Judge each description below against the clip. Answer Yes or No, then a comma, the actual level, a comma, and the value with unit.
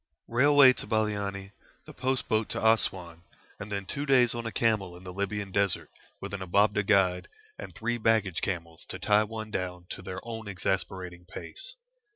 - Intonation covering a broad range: No, average, 3.2 semitones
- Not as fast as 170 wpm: No, average, 180 wpm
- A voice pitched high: No, low, 100 Hz